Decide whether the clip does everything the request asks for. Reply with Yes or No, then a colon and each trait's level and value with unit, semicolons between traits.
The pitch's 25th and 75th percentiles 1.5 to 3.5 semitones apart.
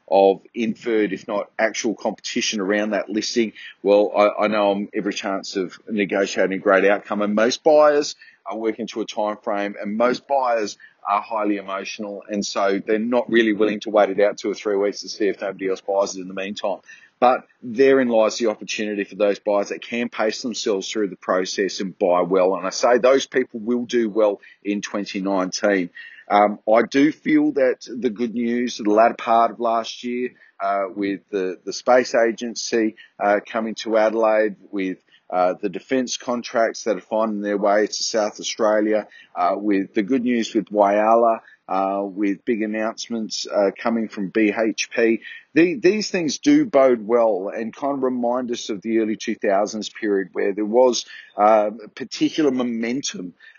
Yes: average, 2.9 semitones